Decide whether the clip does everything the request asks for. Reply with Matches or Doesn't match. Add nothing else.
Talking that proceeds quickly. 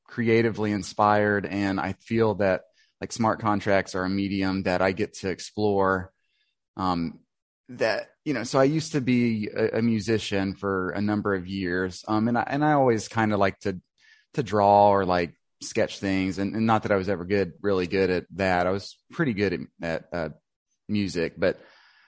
Doesn't match